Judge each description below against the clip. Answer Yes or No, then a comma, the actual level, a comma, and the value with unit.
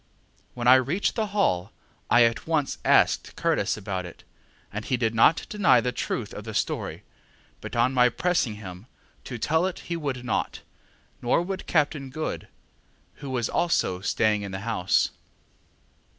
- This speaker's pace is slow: No, average, 165 wpm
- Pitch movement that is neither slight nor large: No, wide, 6.4 semitones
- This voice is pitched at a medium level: No, low, 125 Hz